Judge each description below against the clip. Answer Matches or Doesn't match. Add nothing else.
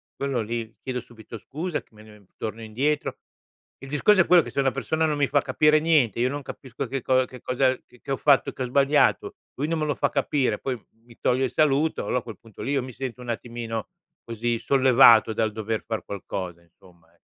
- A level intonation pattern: Doesn't match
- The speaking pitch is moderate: Doesn't match